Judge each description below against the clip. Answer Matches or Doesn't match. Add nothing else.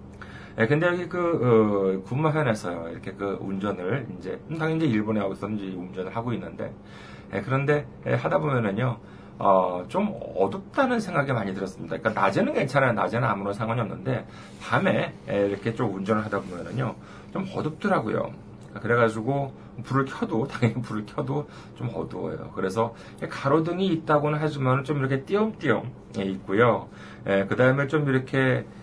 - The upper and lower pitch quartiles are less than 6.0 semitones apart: Doesn't match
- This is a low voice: Matches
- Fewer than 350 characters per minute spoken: Doesn't match